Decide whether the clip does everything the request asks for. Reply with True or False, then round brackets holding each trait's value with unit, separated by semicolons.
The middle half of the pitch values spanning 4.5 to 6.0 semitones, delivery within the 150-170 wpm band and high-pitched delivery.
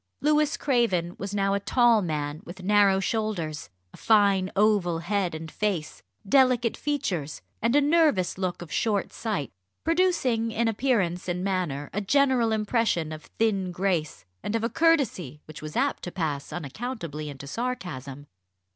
True (5.6 semitones; 155 wpm; 195 Hz)